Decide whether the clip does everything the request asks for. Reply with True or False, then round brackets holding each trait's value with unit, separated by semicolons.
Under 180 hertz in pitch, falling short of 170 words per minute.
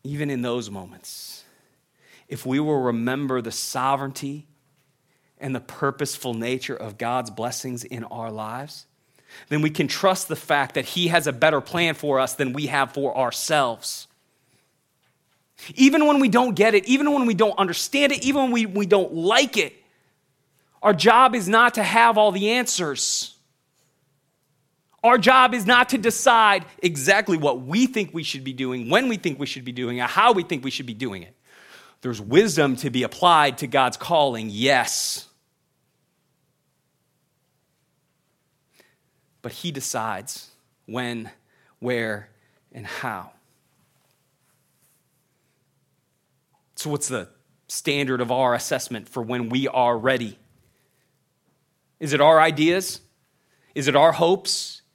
True (140 Hz; 145 wpm)